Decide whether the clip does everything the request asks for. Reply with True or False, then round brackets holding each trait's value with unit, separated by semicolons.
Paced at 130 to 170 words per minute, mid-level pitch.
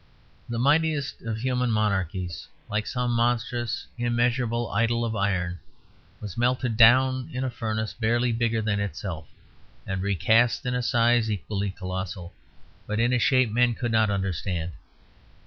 False (145 wpm; 115 Hz)